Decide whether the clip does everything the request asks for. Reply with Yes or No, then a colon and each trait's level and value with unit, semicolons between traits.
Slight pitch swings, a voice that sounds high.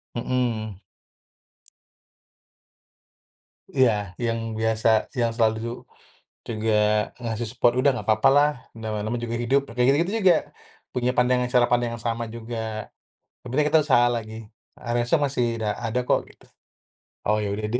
No: narrow, 2.1 semitones; low, 120 Hz